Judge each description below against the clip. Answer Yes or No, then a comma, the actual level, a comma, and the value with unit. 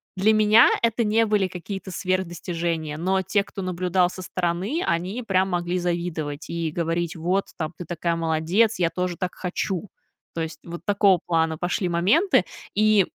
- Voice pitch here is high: No, medium, 180 Hz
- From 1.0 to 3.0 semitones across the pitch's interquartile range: Yes, average, 2.7 semitones